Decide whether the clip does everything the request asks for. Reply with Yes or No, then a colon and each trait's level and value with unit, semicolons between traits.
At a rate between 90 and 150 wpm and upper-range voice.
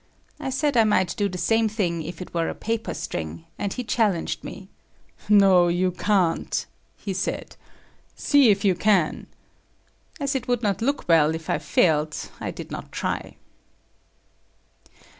No: average, 160 wpm; high, 195 Hz